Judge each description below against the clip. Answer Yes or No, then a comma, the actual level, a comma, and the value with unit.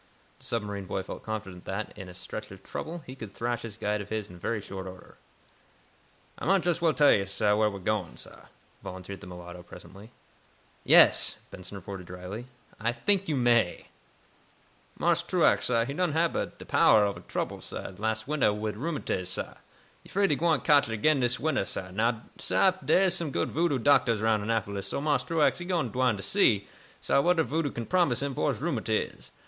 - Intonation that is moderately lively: No, wide, 6.8 semitones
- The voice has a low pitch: Yes, low, 115 Hz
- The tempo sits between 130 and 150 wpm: No, average, 200 wpm